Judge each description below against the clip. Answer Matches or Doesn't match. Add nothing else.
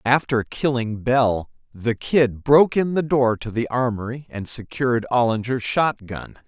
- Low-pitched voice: Matches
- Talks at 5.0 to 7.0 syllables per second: Doesn't match